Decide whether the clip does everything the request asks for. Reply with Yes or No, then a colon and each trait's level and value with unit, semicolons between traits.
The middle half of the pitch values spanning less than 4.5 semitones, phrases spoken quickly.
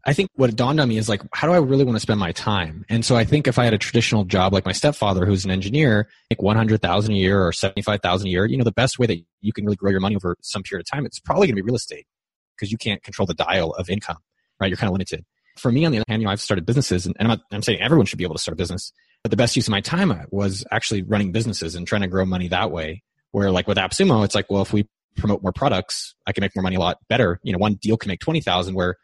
Yes: average, 3.3 semitones; fast, 315 wpm